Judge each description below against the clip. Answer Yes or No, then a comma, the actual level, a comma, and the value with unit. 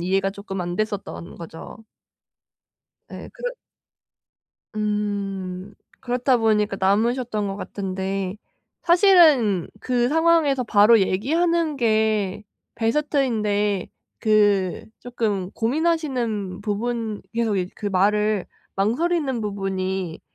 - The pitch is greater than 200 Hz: Yes, high, 210 Hz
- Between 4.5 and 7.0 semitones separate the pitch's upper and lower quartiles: No, average, 4.1 semitones